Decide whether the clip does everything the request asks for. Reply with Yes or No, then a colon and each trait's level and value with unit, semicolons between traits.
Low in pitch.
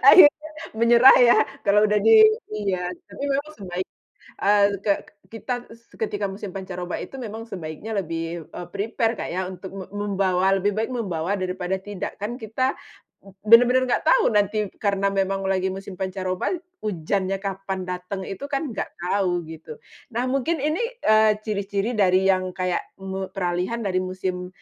No: high, 200 Hz